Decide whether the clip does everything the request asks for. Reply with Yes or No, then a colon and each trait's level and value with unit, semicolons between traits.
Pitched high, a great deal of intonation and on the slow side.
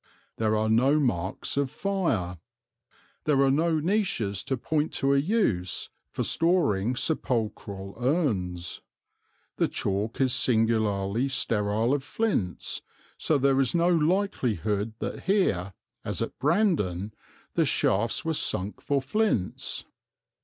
No: low, 125 Hz; wide, 7.3 semitones; slow, 125 wpm